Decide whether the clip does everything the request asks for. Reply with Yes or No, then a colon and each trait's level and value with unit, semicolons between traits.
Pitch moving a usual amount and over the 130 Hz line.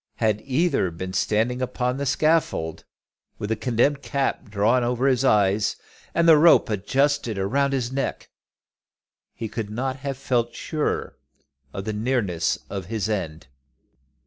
No: average, 4.6 semitones; low, 120 Hz